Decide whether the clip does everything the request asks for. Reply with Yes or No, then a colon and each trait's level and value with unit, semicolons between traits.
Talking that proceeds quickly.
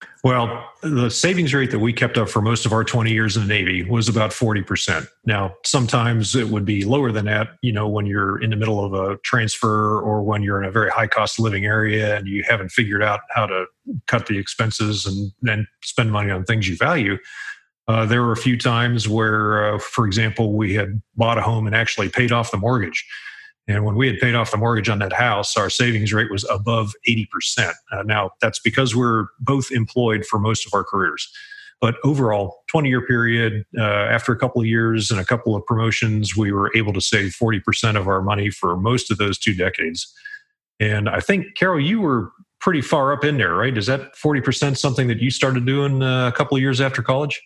Yes: fast, 220 wpm